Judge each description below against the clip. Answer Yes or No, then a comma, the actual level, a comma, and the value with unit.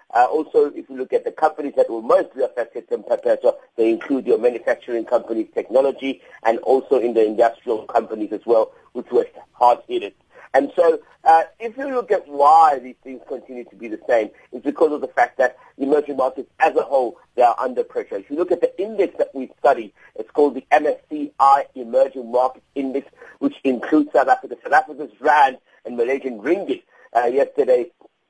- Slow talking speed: No, average, 190 wpm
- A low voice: No, very high, 295 Hz